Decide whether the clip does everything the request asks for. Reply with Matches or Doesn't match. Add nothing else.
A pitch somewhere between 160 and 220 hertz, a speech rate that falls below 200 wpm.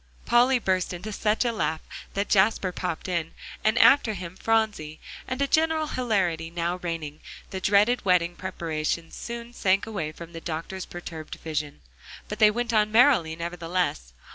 Matches